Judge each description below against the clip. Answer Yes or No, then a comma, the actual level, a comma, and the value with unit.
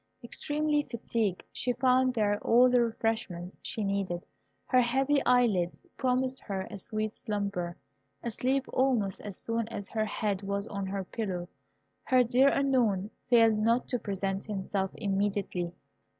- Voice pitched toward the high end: Yes, high, 220 Hz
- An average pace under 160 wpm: Yes, average, 140 wpm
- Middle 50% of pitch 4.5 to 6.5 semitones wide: No, average, 4.1 semitones